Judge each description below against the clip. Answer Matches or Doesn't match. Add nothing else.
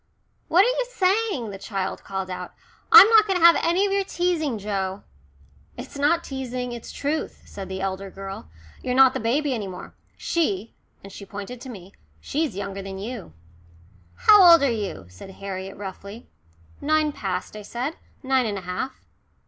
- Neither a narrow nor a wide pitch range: Doesn't match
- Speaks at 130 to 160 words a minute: Doesn't match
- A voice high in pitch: Matches